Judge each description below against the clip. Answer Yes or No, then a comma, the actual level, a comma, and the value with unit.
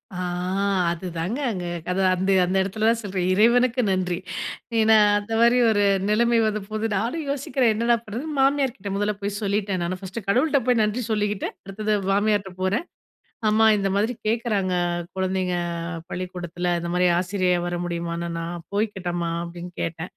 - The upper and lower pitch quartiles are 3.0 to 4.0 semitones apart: Yes, average, 3.6 semitones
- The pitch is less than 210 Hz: Yes, high, 200 Hz